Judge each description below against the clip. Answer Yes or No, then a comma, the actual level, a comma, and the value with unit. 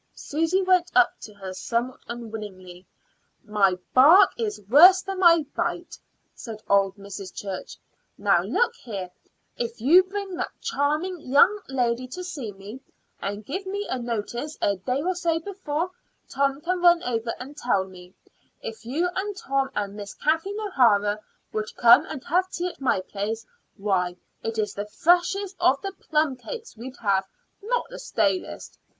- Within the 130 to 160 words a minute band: Yes, average, 155 wpm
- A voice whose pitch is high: Yes, very high, 260 Hz